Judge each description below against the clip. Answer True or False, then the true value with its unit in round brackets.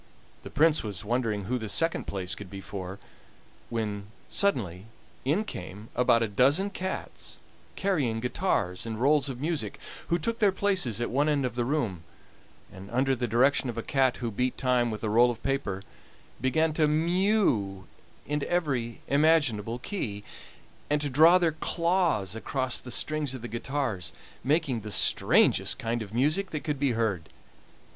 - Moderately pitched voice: False (125 Hz)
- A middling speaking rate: True (165 wpm)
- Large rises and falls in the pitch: True (5.8 semitones)